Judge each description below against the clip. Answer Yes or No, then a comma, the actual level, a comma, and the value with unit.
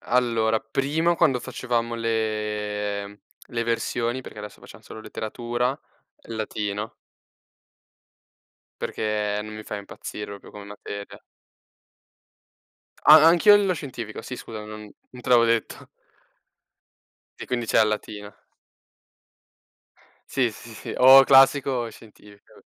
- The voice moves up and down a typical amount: Yes, average, 3.0 semitones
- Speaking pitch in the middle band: No, low, 115 Hz